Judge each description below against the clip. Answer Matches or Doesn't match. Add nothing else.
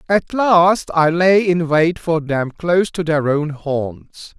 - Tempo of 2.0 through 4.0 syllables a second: Matches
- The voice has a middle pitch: Matches